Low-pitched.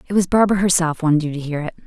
No: medium, 170 Hz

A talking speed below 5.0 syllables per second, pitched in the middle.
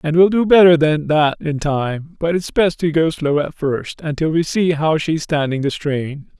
Yes: 4.6 syllables/s; medium, 155 Hz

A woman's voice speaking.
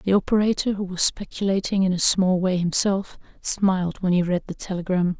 Yes: female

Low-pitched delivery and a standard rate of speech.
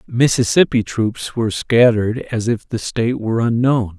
Yes: low, 115 Hz; average, 150 wpm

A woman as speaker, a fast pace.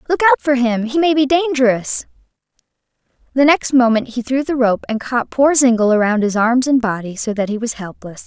Yes: female; fast, 210 wpm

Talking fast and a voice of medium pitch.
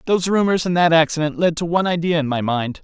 Yes: fast, 255 wpm; medium, 165 Hz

